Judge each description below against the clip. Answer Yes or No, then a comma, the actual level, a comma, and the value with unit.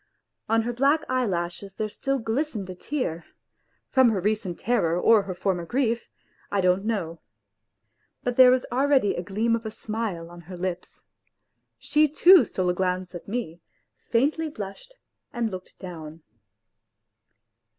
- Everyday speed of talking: Yes, average, 150 wpm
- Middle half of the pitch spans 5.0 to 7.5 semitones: Yes, wide, 5.5 semitones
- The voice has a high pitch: Yes, high, 215 Hz